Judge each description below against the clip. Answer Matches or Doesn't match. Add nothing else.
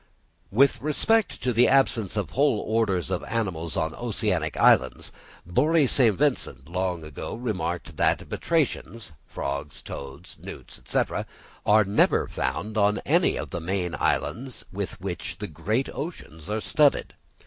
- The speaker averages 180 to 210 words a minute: Doesn't match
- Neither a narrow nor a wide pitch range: Doesn't match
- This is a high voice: Doesn't match